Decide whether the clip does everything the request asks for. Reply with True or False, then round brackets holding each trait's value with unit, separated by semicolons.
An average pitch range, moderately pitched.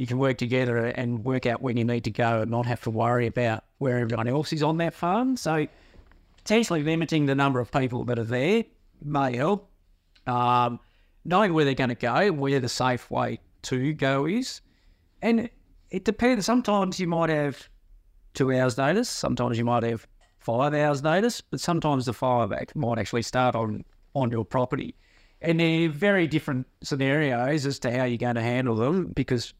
False (4.9 semitones; 130 Hz)